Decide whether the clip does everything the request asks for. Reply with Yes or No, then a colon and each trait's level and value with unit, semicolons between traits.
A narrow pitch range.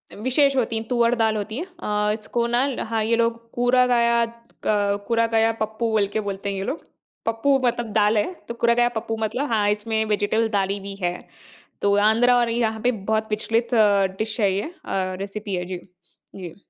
Yes: narrow, 2.2 semitones